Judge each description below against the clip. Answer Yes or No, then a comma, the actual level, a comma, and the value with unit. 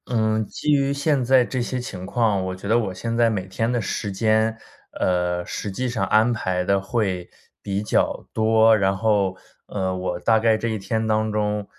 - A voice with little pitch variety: No, average, 3.0 semitones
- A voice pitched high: No, low, 110 Hz